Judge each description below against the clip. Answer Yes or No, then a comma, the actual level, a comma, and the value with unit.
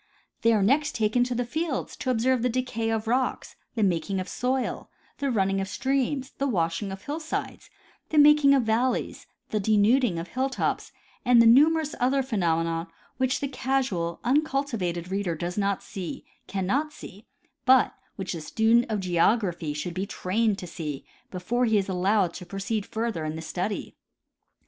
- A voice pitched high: Yes, high, 220 Hz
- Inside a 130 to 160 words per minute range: No, average, 170 wpm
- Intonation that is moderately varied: No, wide, 5.7 semitones